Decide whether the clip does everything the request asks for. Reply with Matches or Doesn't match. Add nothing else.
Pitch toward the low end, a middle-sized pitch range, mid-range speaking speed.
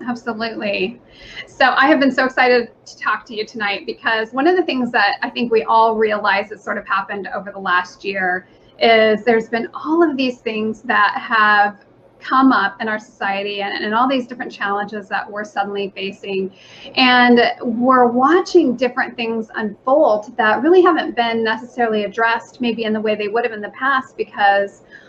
Doesn't match